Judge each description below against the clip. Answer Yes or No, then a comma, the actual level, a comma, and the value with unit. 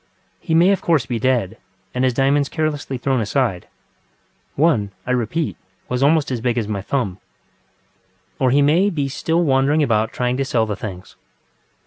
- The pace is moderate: Yes, average, 165 wpm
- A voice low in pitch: Yes, low, 130 Hz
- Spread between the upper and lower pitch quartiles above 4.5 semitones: No, average, 4.2 semitones